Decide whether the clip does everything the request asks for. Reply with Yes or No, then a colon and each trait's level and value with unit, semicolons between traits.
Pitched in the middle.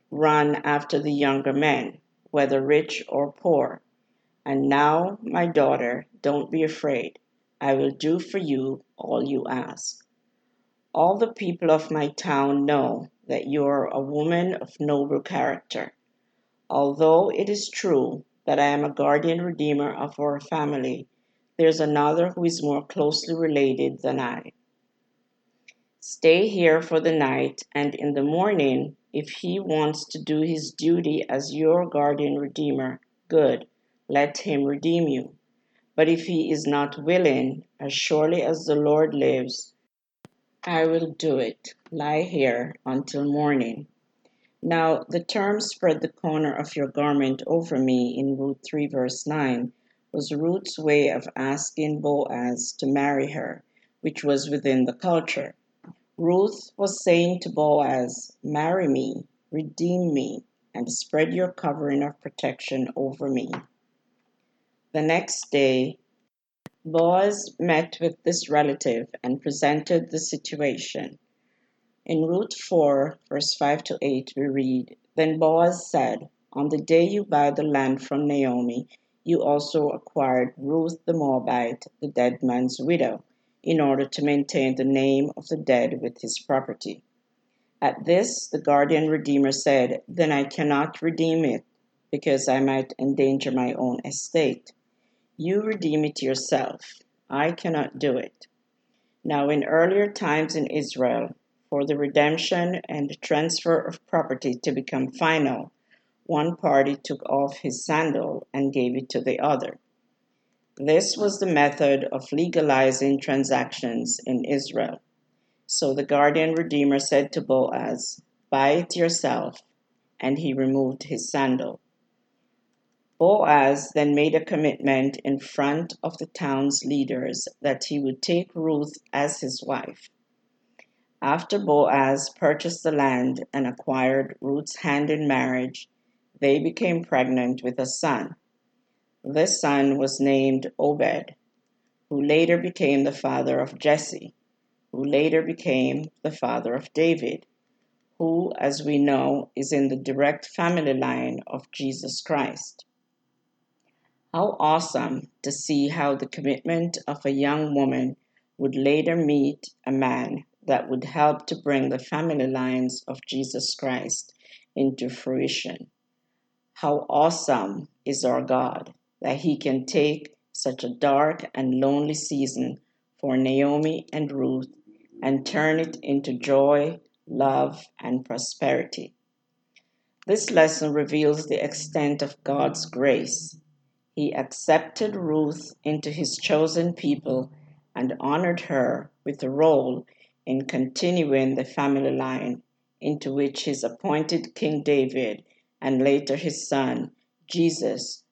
Yes: medium, 145 Hz